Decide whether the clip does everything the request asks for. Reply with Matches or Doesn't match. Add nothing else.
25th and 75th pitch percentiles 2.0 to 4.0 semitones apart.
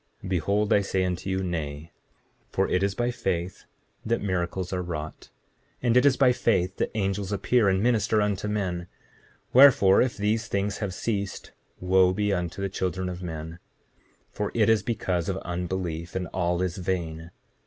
Matches